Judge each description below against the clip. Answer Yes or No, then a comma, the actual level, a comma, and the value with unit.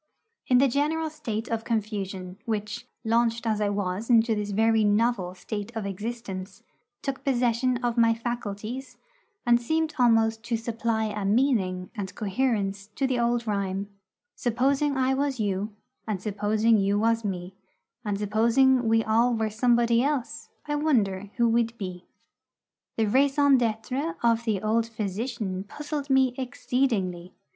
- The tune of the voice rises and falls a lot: No, average, 3.3 semitones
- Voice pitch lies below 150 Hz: No, high, 225 Hz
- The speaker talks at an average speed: Yes, average, 145 wpm